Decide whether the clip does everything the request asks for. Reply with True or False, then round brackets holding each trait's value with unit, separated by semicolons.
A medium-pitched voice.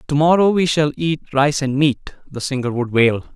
True (145 Hz)